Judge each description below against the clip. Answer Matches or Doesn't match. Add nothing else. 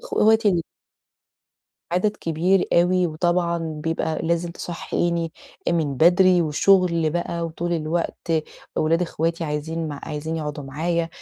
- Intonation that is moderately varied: Doesn't match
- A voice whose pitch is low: Doesn't match